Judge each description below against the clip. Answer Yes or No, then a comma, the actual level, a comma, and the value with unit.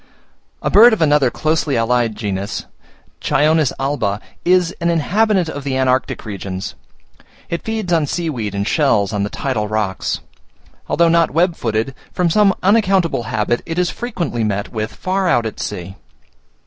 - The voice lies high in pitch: No, medium, 140 Hz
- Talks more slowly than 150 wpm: No, average, 160 wpm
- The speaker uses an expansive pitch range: Yes, wide, 8.1 semitones